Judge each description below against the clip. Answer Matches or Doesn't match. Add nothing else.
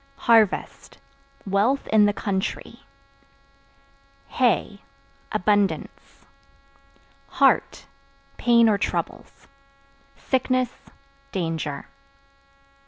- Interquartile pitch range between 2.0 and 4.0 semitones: Matches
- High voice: Matches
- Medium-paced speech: Doesn't match